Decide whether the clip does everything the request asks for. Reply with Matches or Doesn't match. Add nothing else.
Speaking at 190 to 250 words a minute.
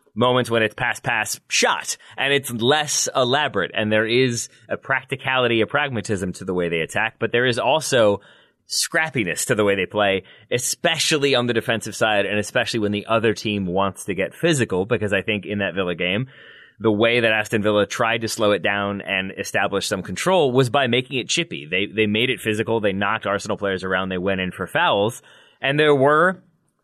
Matches